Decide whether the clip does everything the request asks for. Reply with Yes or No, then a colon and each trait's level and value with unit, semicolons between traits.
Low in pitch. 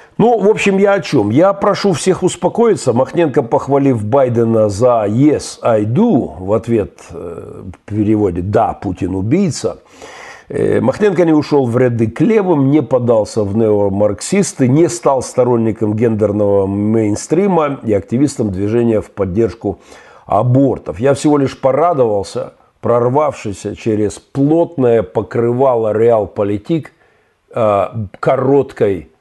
Yes: low, 120 Hz